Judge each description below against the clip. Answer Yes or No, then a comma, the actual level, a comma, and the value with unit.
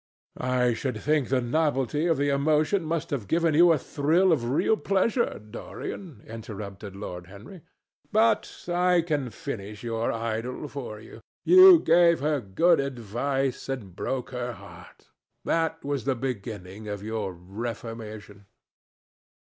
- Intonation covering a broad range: Yes, wide, 6.5 semitones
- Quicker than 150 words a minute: No, average, 140 wpm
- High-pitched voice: No, low, 130 Hz